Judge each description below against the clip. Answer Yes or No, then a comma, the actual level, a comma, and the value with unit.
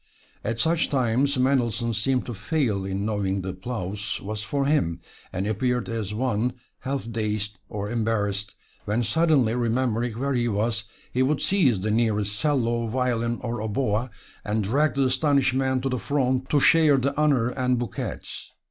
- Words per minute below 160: No, average, 165 wpm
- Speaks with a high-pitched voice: No, low, 120 Hz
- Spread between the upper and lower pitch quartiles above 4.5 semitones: No, average, 3.8 semitones